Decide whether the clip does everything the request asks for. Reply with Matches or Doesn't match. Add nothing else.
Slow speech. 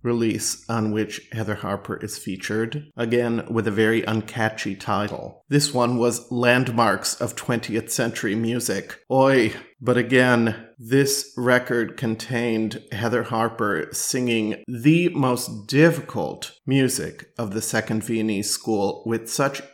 Matches